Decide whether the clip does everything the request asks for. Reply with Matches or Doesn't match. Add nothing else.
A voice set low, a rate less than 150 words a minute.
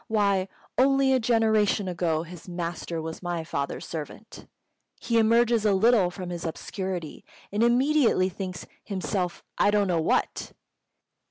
Doesn't match